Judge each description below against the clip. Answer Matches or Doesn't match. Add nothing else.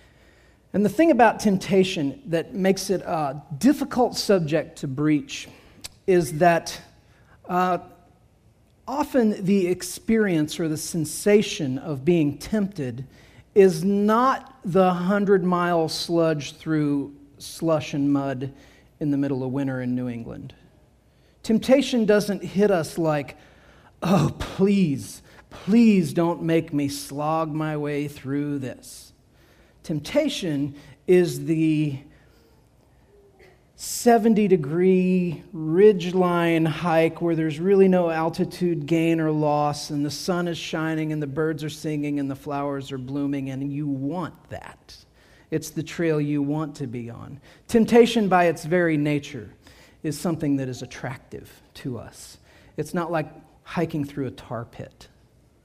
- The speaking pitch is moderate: Matches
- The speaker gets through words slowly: Matches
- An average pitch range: Matches